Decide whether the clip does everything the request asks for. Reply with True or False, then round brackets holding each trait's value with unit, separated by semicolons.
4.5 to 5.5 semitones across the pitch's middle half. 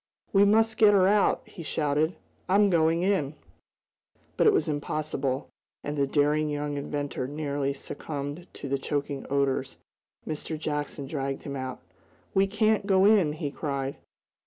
True (5.1 semitones)